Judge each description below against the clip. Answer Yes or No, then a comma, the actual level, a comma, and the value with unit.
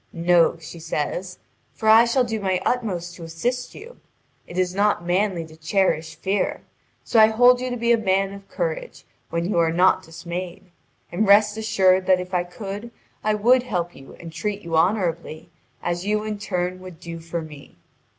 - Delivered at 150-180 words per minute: No, average, 190 wpm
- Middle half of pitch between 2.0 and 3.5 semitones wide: No, average, 4.0 semitones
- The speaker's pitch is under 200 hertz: Yes, medium, 185 Hz